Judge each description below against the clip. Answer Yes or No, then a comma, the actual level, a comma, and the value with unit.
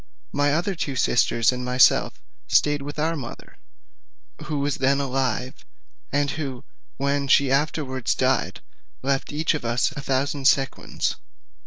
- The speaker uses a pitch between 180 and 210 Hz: No, medium, 140 Hz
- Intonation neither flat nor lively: No, narrow, 2.0 semitones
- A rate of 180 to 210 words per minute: No, average, 140 wpm